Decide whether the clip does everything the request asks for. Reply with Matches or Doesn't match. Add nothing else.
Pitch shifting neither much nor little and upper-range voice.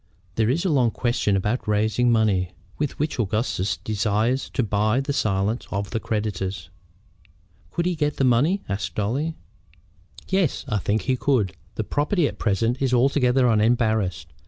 Doesn't match